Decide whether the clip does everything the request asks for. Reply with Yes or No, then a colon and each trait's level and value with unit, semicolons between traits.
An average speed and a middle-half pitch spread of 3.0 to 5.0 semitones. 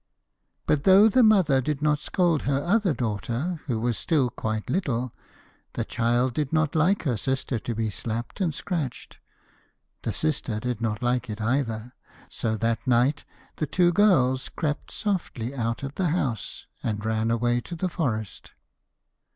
No: average, 160 wpm; wide, 5.4 semitones